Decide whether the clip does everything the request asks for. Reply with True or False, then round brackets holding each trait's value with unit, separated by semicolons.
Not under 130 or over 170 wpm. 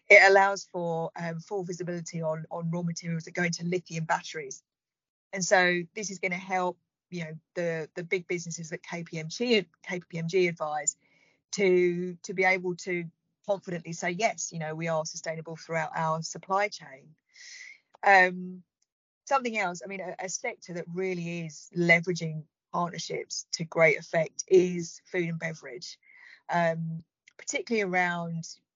True (150 wpm)